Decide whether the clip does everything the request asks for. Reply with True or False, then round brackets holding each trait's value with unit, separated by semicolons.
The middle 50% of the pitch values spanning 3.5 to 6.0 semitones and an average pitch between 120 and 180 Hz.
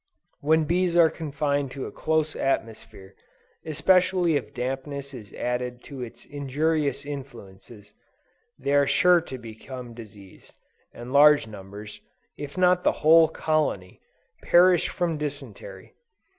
True (4.8 semitones; 140 Hz)